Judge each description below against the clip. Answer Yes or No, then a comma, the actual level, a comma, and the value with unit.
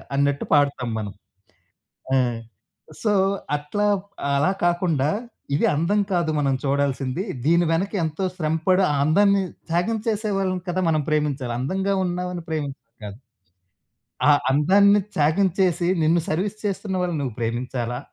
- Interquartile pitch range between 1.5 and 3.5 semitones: No, average, 4.9 semitones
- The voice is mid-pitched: Yes, medium, 160 Hz